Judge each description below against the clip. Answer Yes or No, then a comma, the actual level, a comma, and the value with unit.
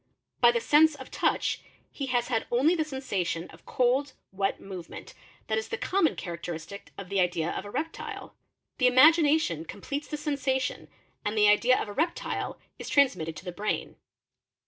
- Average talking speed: Yes, average, 175 wpm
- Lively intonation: Yes, wide, 6.9 semitones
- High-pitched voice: Yes, high, 240 Hz